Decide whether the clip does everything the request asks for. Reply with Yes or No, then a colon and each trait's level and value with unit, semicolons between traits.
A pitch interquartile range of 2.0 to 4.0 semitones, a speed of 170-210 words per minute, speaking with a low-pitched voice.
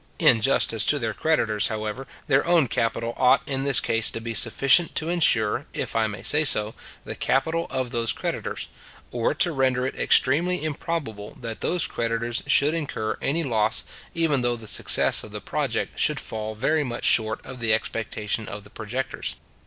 No: average, 4.7 semitones; average, 180 wpm; low, 120 Hz